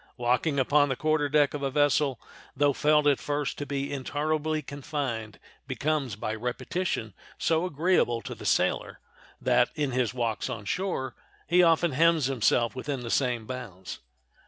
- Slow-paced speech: No, average, 160 wpm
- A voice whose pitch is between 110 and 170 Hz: Yes, medium, 140 Hz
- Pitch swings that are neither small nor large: Yes, average, 3.5 semitones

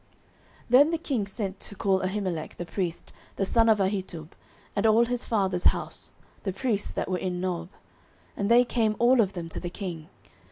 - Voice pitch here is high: Yes, high, 200 Hz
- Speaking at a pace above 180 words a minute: Yes, average, 195 wpm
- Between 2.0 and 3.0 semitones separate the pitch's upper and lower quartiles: No, average, 3.9 semitones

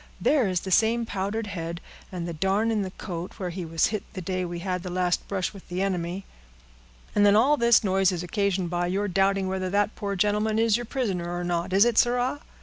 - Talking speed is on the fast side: Yes, fast, 230 wpm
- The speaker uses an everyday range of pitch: Yes, average, 3.1 semitones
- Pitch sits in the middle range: No, high, 195 Hz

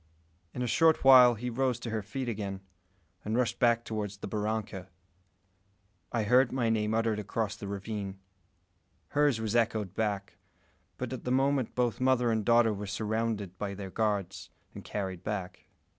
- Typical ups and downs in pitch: Yes, average, 3.0 semitones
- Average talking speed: Yes, average, 165 wpm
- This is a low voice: Yes, low, 110 Hz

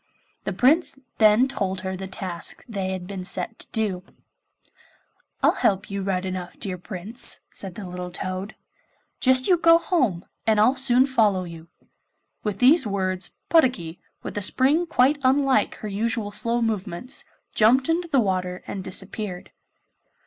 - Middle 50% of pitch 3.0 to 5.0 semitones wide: No, wide, 5.5 semitones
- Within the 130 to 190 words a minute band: Yes, average, 155 wpm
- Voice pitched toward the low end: No, high, 205 Hz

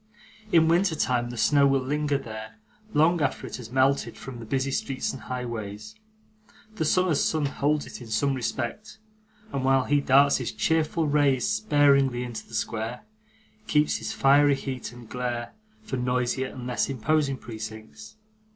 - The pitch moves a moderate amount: Yes, average, 3.4 semitones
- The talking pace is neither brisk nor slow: Yes, average, 160 wpm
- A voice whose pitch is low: Yes, low, 130 Hz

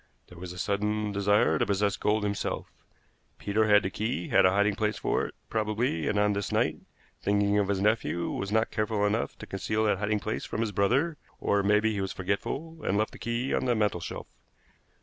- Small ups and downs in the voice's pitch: Yes, narrow, 1.5 semitones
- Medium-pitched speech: No, low, 105 Hz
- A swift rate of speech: Yes, fast, 215 wpm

